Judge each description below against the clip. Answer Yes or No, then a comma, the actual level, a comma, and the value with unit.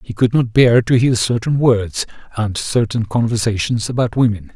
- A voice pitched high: No, low, 115 Hz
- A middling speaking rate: Yes, average, 170 wpm